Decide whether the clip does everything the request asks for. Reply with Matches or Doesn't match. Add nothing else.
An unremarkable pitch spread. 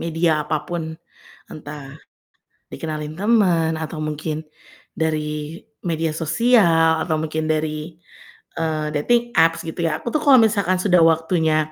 Doesn't match